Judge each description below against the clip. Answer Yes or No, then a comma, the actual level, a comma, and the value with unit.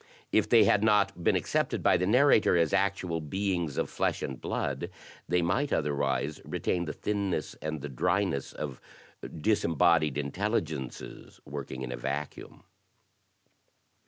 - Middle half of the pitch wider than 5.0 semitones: Yes, wide, 5.5 semitones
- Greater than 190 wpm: No, average, 140 wpm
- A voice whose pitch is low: Yes, very low, 85 Hz